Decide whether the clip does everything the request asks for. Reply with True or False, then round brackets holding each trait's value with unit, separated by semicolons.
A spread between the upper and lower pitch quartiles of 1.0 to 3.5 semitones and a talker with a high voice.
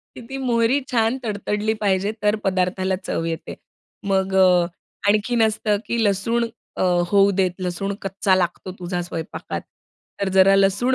True (2.8 semitones; 200 Hz)